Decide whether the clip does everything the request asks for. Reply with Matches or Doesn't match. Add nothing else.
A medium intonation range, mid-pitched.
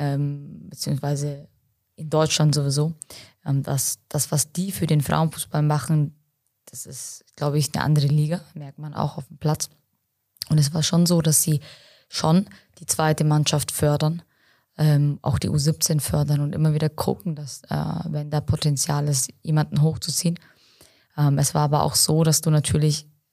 Doesn't match